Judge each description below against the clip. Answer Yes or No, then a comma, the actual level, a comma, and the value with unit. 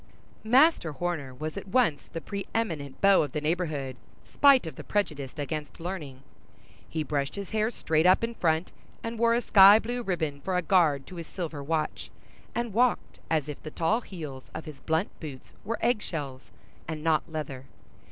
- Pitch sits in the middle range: Yes, medium, 165 Hz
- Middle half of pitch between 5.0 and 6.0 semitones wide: Yes, average, 5.3 semitones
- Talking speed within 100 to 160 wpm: No, average, 180 wpm